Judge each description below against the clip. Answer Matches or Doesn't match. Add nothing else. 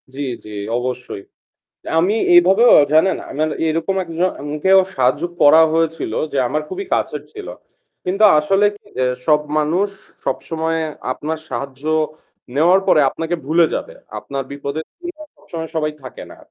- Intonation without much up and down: Doesn't match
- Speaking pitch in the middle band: Matches